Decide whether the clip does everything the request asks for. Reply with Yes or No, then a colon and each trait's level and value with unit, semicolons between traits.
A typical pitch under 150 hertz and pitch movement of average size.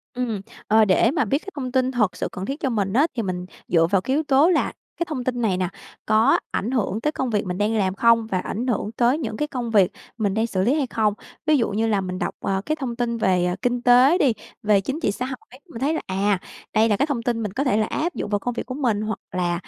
No: high, 230 Hz; average, 4.3 semitones